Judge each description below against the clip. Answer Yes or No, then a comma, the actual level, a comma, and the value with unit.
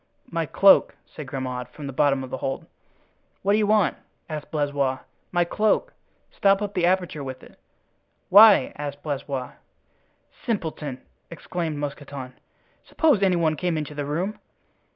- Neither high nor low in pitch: Yes, medium, 155 Hz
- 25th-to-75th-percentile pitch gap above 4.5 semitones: Yes, average, 5.1 semitones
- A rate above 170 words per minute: No, average, 145 wpm